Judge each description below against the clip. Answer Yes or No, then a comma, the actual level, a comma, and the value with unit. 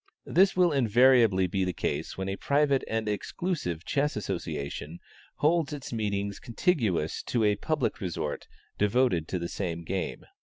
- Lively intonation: Yes, wide, 7.1 semitones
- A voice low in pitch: Yes, low, 105 Hz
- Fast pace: No, average, 150 wpm